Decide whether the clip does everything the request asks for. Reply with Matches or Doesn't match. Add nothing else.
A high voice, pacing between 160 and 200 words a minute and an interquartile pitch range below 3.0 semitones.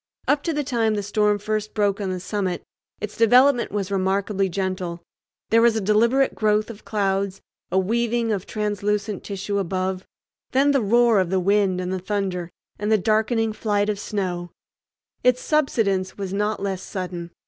Matches